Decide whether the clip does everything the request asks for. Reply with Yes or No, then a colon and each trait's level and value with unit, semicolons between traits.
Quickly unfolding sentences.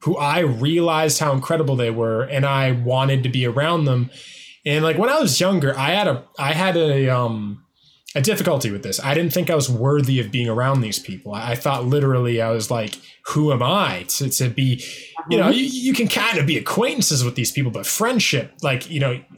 Yes: fast, 220 wpm